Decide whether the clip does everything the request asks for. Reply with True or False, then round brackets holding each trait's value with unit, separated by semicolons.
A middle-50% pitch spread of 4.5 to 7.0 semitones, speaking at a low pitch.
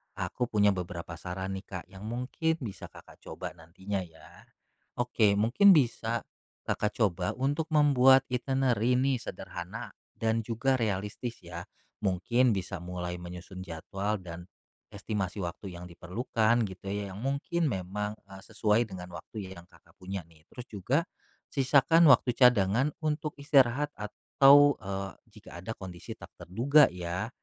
True (5.3 semitones; 105 Hz)